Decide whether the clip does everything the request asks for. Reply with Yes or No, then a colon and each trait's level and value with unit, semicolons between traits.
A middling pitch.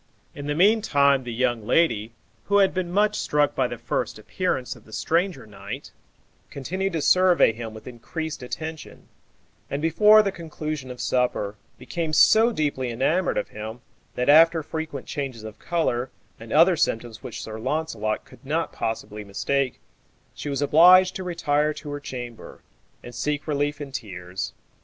Yes: medium, 145 Hz